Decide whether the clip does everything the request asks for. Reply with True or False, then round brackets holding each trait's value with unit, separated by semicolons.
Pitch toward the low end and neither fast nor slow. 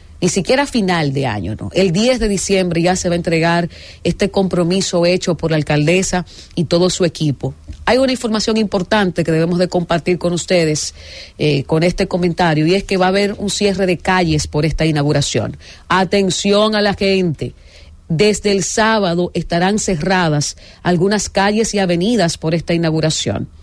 False (175 Hz; 175 wpm)